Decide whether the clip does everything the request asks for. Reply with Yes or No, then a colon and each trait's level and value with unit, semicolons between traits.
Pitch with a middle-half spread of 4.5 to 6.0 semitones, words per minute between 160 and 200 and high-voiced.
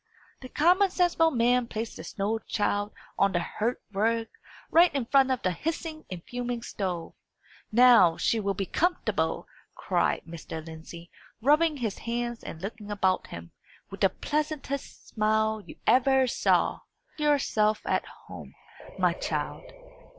No: wide, 5.6 semitones; average, 145 wpm; high, 230 Hz